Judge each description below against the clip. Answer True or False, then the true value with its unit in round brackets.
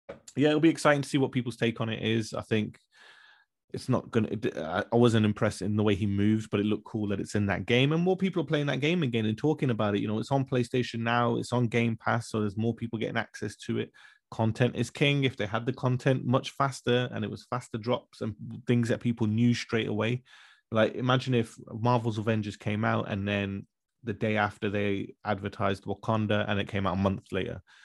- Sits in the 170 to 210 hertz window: False (115 Hz)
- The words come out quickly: True (235 wpm)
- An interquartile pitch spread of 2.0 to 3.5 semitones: True (2.9 semitones)